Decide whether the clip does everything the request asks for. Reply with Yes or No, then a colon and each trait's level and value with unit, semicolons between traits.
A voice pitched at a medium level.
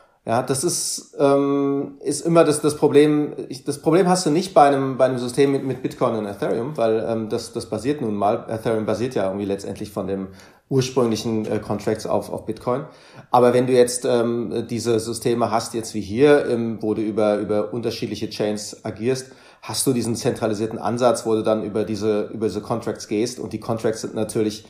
No: low, 115 Hz